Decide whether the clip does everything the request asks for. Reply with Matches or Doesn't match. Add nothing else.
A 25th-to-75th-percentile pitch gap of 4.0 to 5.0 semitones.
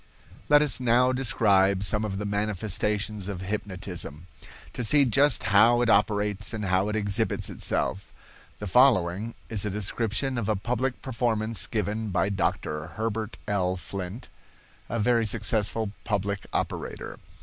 Doesn't match